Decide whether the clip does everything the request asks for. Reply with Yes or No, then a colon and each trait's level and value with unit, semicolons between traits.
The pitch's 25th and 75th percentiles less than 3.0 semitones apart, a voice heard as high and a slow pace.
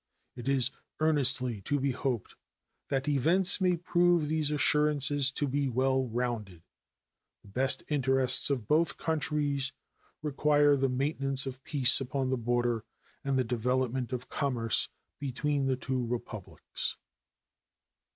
No: narrow, 2.6 semitones; low, 135 Hz; slow, 130 wpm